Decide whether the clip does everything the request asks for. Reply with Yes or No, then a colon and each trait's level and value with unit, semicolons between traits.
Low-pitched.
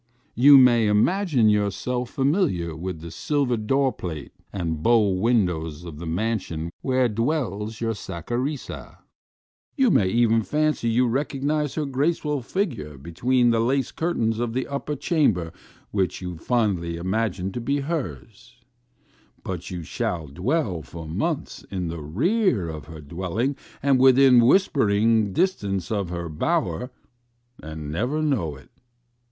Yes: low, 115 Hz